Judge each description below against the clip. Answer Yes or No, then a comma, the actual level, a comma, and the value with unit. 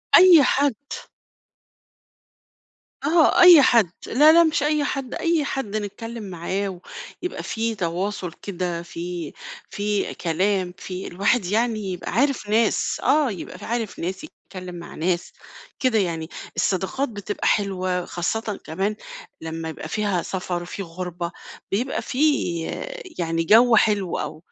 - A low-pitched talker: No, high, 200 Hz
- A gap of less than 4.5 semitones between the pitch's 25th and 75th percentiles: No, wide, 5.5 semitones